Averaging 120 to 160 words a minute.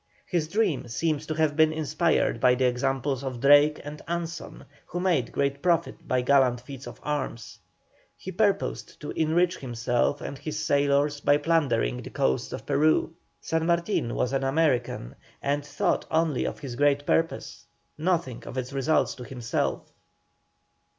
Yes: average, 155 wpm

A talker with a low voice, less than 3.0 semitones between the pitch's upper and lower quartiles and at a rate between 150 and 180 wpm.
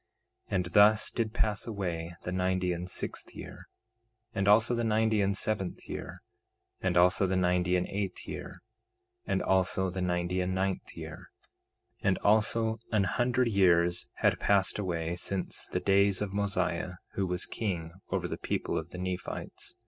Yes: very low, 95 Hz; narrow, 2.4 semitones; average, 165 wpm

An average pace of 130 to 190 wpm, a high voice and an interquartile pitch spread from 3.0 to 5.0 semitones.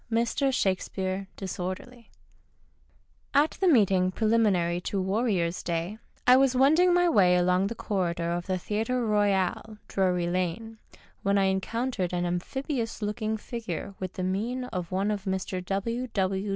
Yes: average, 150 wpm; high, 200 Hz; average, 4.0 semitones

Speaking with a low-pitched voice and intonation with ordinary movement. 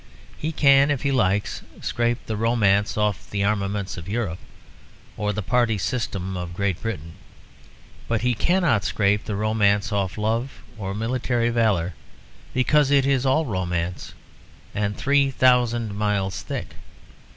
Yes: low, 110 Hz; average, 3.8 semitones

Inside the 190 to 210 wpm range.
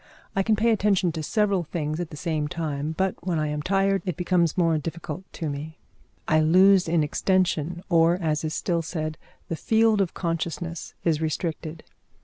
No: average, 180 wpm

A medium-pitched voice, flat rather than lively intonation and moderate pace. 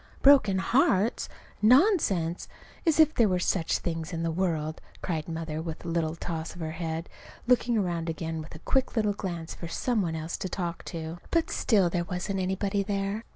No: medium, 175 Hz; average, 4.0 semitones; average, 190 wpm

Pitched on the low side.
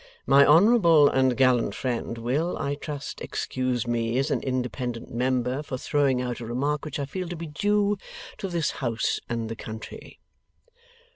Yes: low, 130 Hz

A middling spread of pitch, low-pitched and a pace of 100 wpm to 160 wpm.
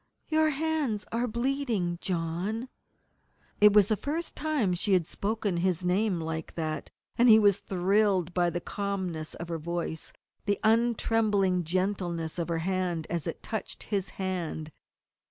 No: average, 4.2 semitones; high, 190 Hz; average, 150 wpm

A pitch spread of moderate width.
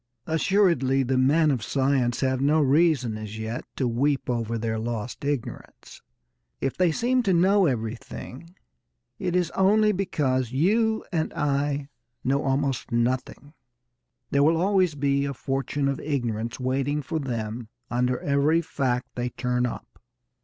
Yes: average, 4.3 semitones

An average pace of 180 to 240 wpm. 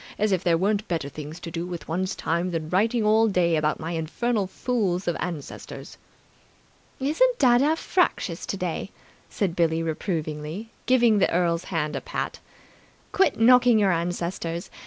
No: average, 155 wpm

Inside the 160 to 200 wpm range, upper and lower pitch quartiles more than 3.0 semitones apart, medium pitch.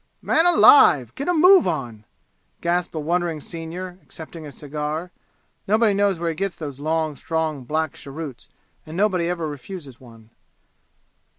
No: average, 150 wpm; average, 3.6 semitones; medium, 160 Hz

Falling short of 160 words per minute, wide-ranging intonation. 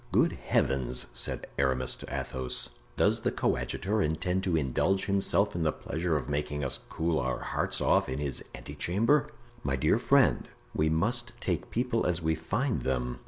No: average, 170 wpm; wide, 6.4 semitones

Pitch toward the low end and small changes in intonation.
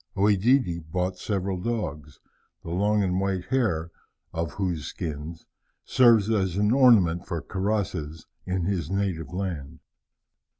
No: very low, 95 Hz; average, 3.5 semitones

